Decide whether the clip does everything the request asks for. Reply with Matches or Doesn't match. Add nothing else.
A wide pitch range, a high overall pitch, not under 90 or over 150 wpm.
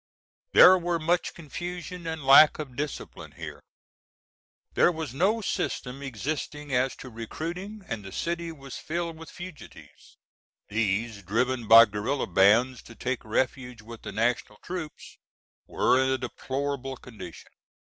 Doesn't match